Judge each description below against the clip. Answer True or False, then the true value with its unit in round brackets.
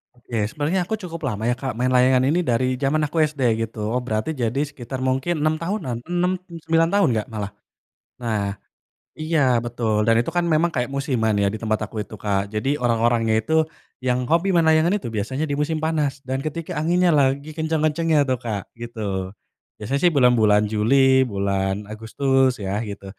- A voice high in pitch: False (130 Hz)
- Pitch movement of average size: False (5.8 semitones)